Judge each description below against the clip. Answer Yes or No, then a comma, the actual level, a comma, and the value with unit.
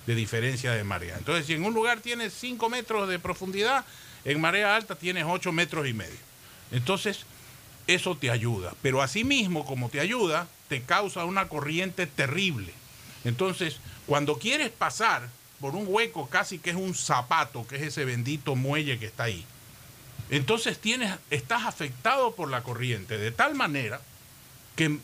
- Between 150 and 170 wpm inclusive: Yes, average, 160 wpm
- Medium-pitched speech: Yes, medium, 150 Hz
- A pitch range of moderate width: No, wide, 7.0 semitones